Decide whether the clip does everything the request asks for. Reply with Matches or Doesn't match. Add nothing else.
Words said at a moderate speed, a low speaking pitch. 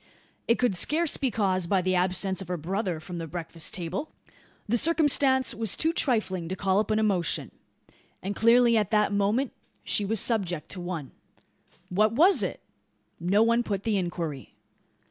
Doesn't match